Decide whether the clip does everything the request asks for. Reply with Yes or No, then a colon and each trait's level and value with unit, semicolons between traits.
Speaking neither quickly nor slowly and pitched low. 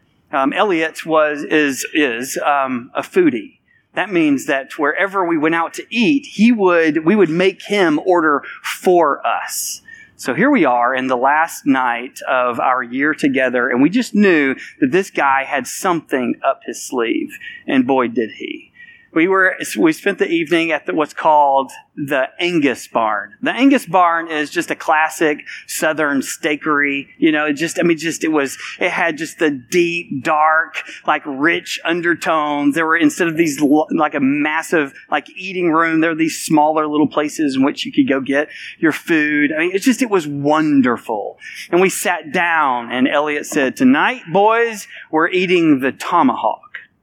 No: average, 175 wpm; medium, 170 Hz